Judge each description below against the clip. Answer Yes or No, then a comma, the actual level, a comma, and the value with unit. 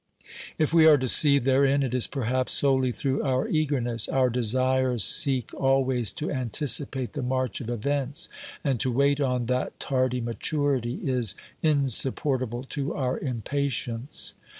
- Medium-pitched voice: No, low, 130 Hz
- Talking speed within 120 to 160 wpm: Yes, average, 140 wpm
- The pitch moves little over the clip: Yes, narrow, 2.1 semitones